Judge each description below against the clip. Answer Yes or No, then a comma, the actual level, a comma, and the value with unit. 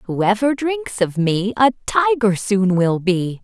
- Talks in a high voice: Yes, high, 220 Hz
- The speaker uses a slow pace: No, average, 155 wpm